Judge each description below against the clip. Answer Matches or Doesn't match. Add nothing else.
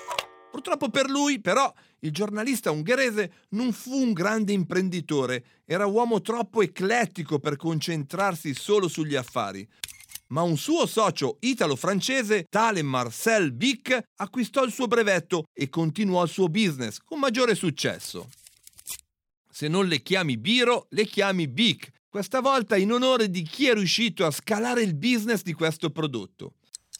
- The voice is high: Matches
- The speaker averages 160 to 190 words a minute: Doesn't match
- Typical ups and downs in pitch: Doesn't match